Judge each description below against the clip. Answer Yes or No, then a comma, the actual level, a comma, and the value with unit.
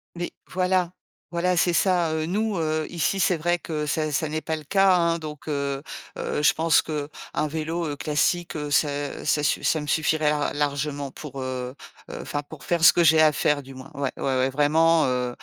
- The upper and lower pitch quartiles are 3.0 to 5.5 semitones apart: No, narrow, 2.6 semitones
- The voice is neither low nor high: Yes, medium, 155 Hz